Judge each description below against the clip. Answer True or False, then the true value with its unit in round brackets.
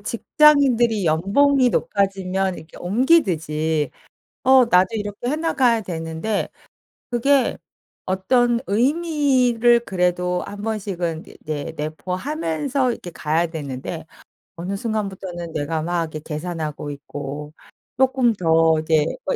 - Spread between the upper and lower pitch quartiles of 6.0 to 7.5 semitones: True (6.9 semitones)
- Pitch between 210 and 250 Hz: False (190 Hz)